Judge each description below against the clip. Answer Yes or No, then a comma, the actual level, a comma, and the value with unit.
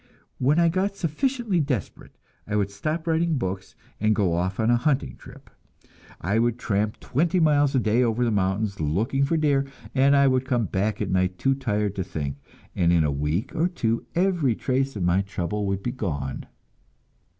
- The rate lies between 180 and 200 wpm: Yes, average, 190 wpm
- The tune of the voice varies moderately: No, wide, 6.6 semitones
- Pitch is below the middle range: Yes, low, 115 Hz